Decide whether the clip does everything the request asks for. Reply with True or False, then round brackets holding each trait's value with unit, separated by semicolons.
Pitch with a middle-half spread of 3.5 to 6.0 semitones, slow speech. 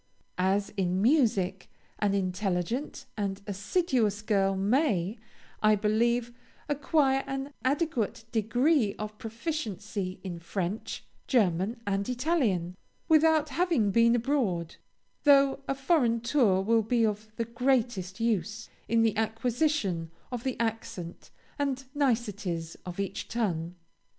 True (5.1 semitones; 115 wpm)